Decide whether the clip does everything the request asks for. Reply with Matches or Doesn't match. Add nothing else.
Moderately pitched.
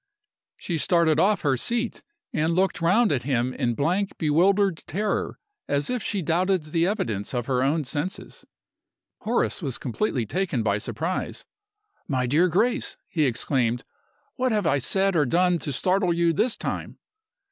Matches